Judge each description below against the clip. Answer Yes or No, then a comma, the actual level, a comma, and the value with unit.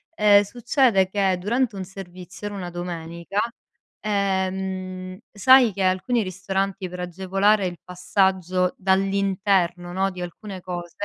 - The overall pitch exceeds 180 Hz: Yes, high, 190 Hz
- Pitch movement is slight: Yes, narrow, 1.7 semitones